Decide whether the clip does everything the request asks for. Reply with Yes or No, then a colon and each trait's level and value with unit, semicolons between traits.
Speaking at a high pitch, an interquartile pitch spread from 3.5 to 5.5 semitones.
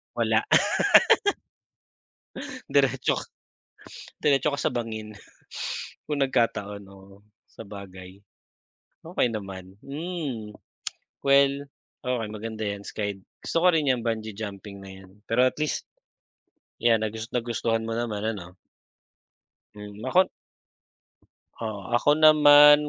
No: low, 115 Hz; average, 5.2 semitones